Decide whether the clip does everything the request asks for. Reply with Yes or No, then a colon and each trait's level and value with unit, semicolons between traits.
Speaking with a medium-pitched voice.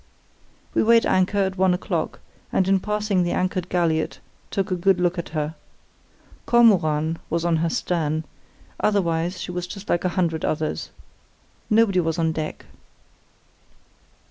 Yes: medium, 180 Hz